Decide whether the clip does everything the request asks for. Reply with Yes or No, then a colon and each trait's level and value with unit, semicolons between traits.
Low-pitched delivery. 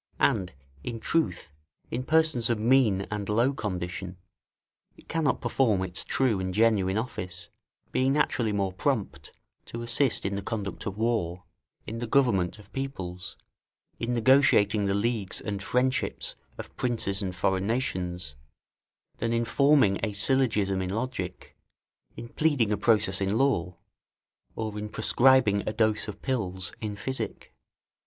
Yes: low, 105 Hz